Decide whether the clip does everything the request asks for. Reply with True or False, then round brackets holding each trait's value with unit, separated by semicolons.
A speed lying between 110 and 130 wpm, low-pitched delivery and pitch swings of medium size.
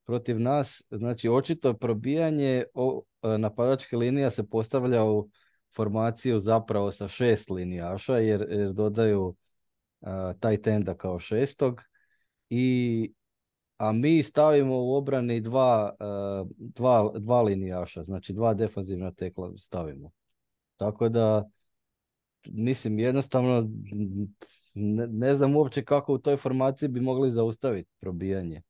True (120 wpm; 115 Hz; 4.2 semitones)